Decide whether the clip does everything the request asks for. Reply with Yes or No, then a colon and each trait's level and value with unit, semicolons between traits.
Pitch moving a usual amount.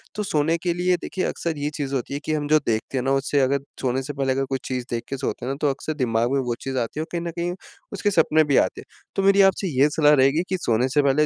Yes: average, 3.6 semitones